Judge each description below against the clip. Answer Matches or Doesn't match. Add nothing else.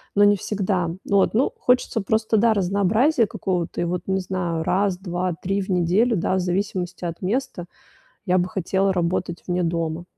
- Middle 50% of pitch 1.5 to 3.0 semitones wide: Matches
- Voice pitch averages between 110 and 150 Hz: Doesn't match